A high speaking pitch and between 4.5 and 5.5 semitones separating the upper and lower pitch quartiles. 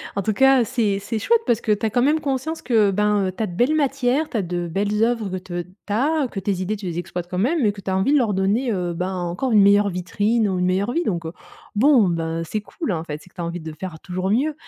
Yes: high, 205 Hz; average, 5.1 semitones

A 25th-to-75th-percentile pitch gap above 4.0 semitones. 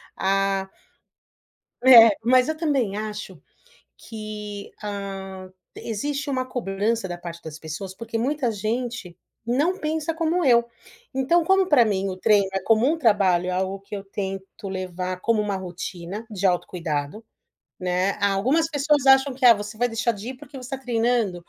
Yes: average, 5.0 semitones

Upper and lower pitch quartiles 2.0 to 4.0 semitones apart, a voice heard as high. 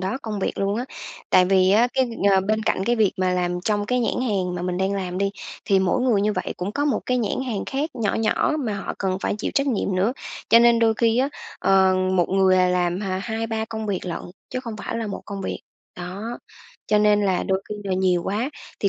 Yes: average, 3.3 semitones; high, 205 Hz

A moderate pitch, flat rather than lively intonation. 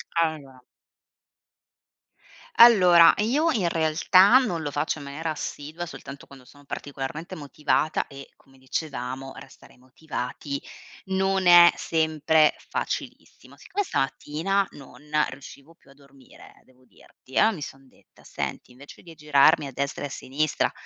No: medium, 150 Hz; average, 3.7 semitones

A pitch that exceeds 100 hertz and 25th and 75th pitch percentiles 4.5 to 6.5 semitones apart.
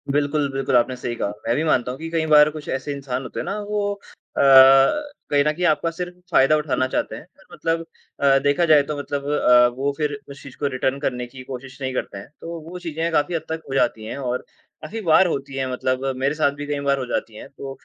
No: medium, 140 Hz; average, 3.4 semitones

